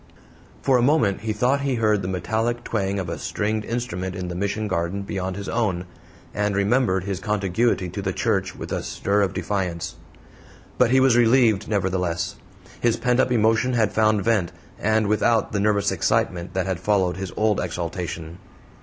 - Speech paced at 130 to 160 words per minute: No, average, 180 wpm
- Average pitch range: Yes, average, 3.4 semitones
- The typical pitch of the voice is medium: No, low, 100 Hz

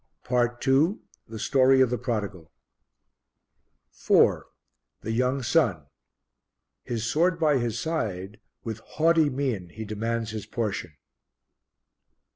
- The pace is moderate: No, slow, 110 wpm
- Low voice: Yes, low, 120 Hz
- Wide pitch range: No, average, 4.0 semitones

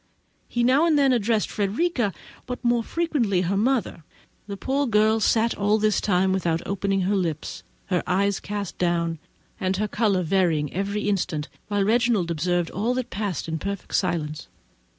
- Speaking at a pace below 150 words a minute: No, average, 160 wpm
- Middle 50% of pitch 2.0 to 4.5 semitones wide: Yes, average, 4.1 semitones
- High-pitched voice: Yes, high, 200 Hz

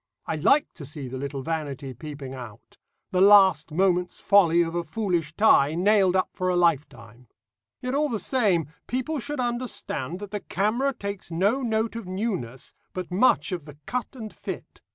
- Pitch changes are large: Yes, wide, 6.3 semitones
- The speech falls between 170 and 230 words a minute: Yes, average, 175 wpm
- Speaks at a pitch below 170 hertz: No, medium, 185 Hz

